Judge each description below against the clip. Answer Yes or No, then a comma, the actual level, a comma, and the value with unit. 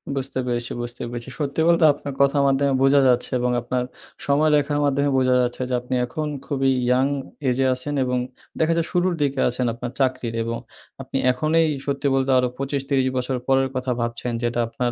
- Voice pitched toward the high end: No, low, 135 Hz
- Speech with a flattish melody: Yes, narrow, 2.2 semitones